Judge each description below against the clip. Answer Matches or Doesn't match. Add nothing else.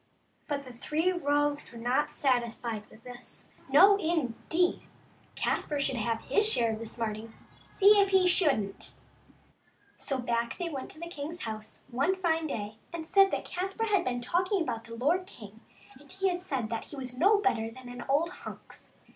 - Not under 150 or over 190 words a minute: Matches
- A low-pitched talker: Doesn't match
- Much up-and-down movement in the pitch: Matches